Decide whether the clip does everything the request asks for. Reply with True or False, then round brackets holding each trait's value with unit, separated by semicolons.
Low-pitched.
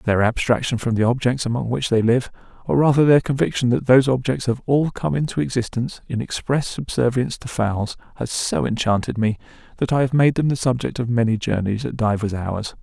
True (120 Hz)